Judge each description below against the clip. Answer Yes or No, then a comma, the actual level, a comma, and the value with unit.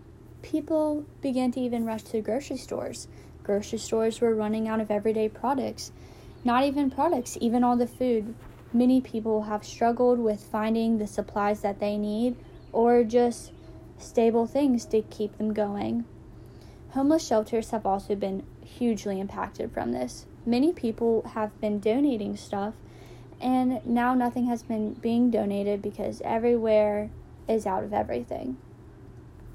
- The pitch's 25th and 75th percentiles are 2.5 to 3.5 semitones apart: Yes, average, 2.9 semitones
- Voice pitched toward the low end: No, high, 220 Hz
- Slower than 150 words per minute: Yes, average, 140 wpm